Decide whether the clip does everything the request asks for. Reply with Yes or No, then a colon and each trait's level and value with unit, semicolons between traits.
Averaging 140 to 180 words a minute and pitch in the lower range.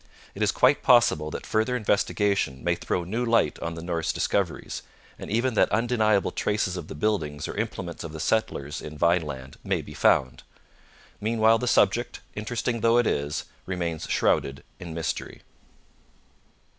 Yes: average, 155 wpm; low, 100 Hz